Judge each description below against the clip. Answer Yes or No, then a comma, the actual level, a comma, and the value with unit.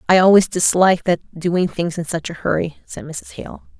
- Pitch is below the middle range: No, medium, 175 Hz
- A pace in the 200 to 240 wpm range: Yes, fast, 205 wpm